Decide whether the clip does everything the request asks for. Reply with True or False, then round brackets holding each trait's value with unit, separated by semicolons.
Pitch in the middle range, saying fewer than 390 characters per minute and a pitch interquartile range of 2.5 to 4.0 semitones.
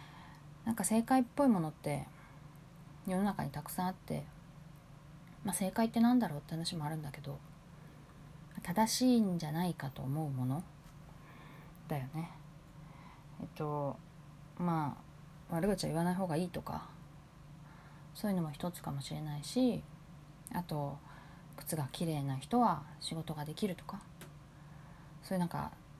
True (155 Hz; 270 characters per minute; 2.9 semitones)